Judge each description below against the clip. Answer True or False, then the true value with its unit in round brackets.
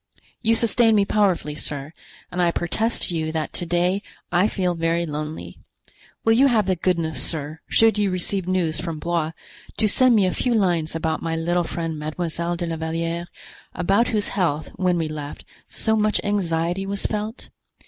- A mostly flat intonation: False (3.9 semitones)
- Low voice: False (175 Hz)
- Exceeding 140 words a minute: True (180 wpm)